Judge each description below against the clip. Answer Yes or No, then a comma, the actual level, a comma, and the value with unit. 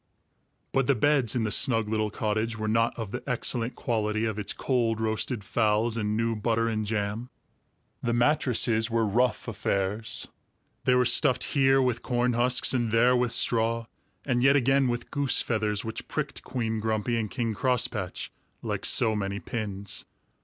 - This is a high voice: No, low, 115 Hz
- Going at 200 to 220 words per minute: No, average, 165 wpm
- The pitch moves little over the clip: Yes, narrow, 2.3 semitones